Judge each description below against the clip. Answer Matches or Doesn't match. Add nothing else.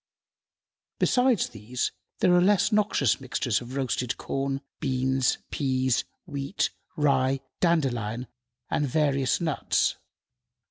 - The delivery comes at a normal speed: Doesn't match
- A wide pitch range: Doesn't match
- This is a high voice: Doesn't match